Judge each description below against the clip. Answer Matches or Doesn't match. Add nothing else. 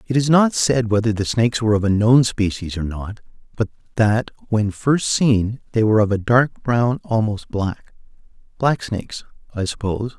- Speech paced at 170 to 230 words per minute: Matches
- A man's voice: Matches